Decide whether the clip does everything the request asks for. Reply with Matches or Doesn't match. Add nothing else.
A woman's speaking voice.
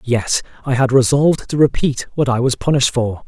Doesn't match